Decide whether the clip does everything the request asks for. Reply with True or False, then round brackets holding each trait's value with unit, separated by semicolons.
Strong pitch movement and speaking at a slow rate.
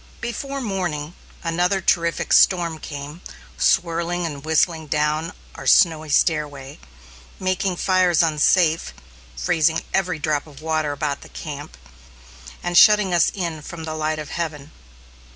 False (2.7 semitones; 130 wpm)